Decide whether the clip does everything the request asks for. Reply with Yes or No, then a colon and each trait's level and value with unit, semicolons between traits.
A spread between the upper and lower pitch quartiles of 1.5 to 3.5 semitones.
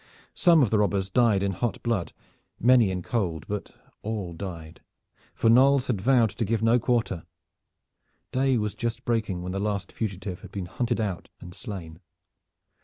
No: average, 4.0 semitones